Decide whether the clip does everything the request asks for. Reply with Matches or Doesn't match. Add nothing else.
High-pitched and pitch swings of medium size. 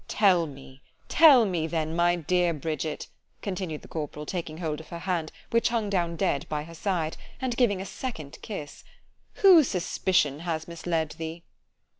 Doesn't match